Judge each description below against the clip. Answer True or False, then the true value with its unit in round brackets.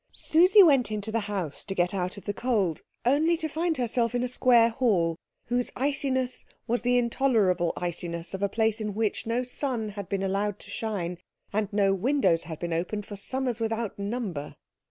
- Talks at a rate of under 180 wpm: False (190 wpm)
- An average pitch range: True (4.4 semitones)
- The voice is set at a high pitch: True (220 Hz)